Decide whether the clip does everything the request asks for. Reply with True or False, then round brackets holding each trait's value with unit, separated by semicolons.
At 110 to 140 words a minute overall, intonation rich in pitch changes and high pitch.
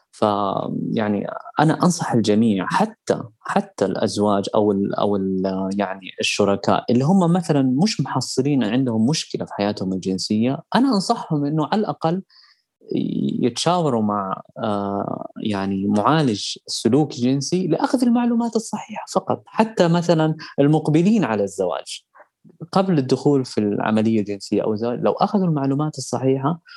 False (120 wpm; 8.6 semitones; 135 Hz)